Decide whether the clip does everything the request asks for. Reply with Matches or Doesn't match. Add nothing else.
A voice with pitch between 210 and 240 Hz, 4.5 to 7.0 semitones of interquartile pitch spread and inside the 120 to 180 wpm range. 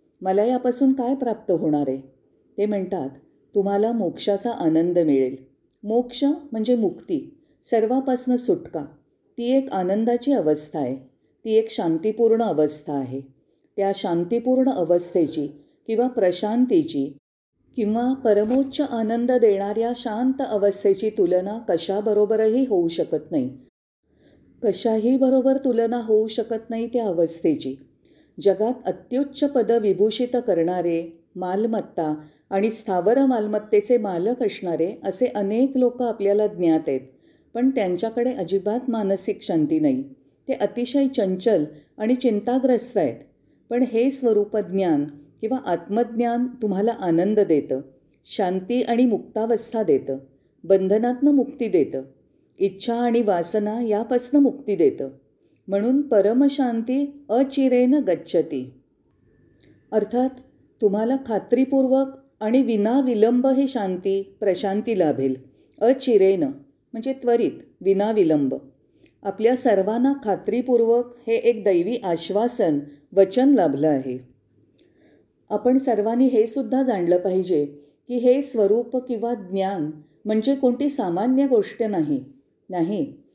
Doesn't match